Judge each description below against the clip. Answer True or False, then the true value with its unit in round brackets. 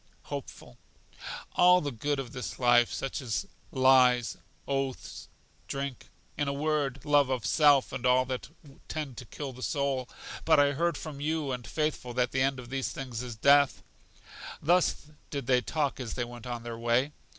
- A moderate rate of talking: True (175 wpm)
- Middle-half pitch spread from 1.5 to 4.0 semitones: True (2.6 semitones)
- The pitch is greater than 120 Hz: True (135 Hz)